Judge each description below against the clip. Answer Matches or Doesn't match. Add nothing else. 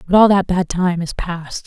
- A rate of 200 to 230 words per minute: Doesn't match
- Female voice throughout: Matches